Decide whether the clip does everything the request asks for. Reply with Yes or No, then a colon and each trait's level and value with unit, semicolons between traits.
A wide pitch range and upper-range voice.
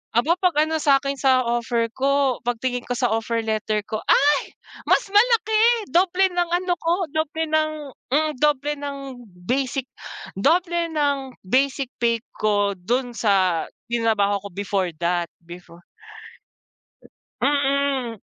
Yes: wide, 5.7 semitones; very high, 270 Hz